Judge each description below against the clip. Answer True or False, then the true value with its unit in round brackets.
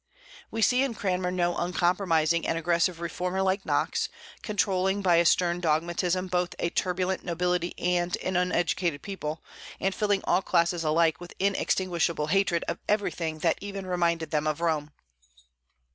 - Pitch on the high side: False (175 Hz)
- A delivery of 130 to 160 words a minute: True (150 wpm)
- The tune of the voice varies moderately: False (2.0 semitones)